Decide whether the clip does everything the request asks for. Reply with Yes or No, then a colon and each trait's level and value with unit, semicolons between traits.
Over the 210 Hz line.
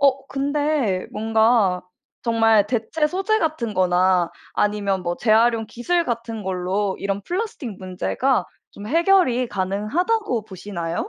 Yes: high, 225 Hz